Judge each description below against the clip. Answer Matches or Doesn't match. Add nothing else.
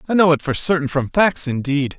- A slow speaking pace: Doesn't match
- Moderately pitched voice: Matches